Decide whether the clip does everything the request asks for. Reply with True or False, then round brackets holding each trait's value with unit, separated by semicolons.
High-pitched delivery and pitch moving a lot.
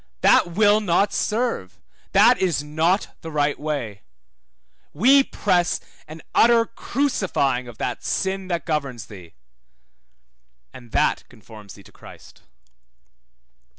False (160 Hz; 8.1 semitones)